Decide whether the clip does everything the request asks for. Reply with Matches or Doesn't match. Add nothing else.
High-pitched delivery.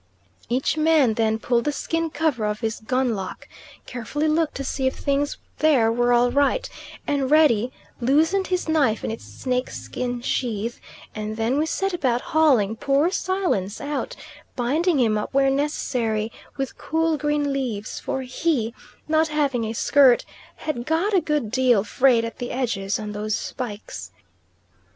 Matches